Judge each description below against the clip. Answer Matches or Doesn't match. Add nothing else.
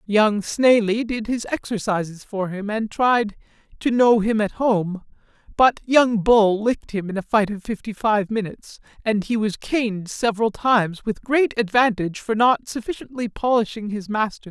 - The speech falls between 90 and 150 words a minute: Doesn't match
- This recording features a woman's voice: Doesn't match